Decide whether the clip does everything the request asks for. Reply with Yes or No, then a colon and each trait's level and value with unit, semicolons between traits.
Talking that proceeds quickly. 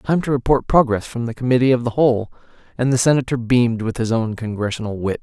Yes: fast, 220 wpm